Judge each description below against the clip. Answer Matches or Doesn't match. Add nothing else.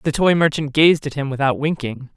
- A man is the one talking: Doesn't match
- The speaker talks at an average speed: Doesn't match